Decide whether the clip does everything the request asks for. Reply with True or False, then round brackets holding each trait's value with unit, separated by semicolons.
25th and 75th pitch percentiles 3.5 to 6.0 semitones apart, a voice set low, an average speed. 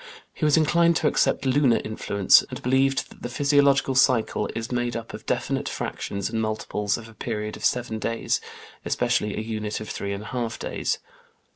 True (3.8 semitones; 115 Hz; 185 wpm)